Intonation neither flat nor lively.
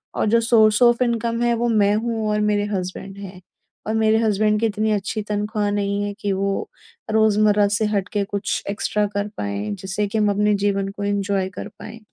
No: narrow, 1.5 semitones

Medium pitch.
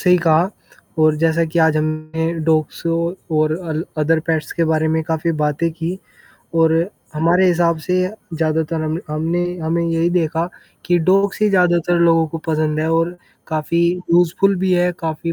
Yes: medium, 165 Hz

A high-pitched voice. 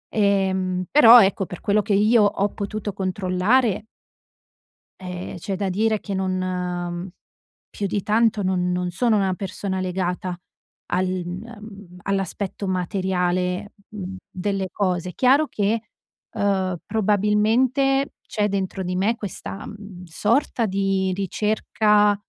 Yes: high, 195 Hz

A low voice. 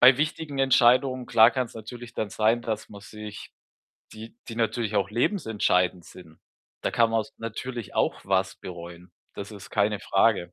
Yes: low, 110 Hz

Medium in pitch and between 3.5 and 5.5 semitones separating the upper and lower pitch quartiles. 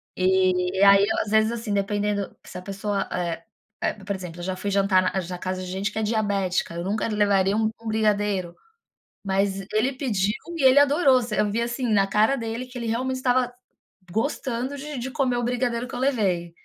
No: high, 210 Hz; average, 4.1 semitones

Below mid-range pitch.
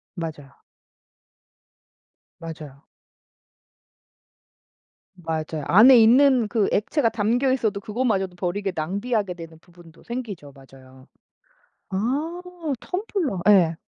No: high, 195 Hz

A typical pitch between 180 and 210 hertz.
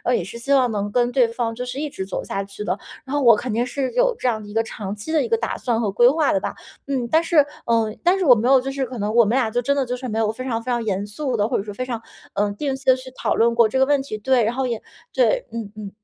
No: high, 240 Hz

